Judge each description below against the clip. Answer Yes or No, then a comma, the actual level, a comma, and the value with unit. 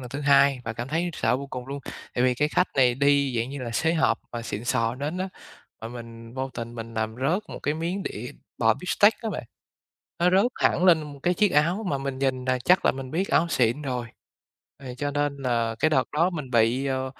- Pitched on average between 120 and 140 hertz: Yes, low, 135 Hz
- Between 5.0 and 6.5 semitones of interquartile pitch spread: No, average, 4.4 semitones